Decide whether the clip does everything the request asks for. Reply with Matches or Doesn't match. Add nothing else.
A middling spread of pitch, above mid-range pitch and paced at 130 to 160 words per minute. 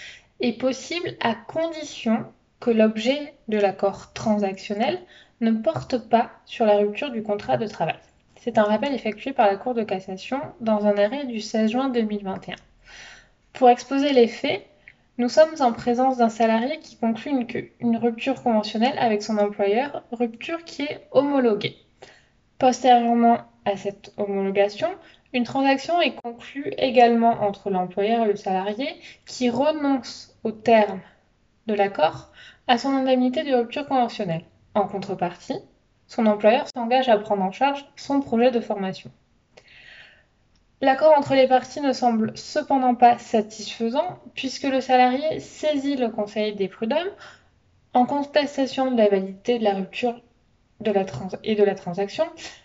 Matches